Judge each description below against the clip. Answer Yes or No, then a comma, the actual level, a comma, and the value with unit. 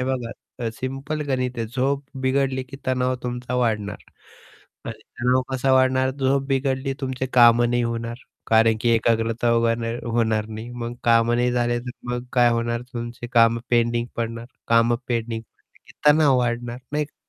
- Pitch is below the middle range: Yes, low, 120 Hz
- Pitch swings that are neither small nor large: No, narrow, 1.9 semitones